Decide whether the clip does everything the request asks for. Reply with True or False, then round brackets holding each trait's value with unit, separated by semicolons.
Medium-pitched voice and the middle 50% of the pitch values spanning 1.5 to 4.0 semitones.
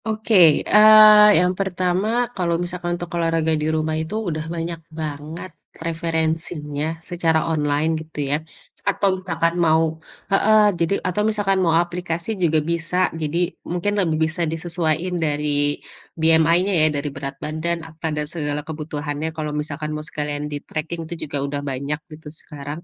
True (160 Hz; 2.5 semitones)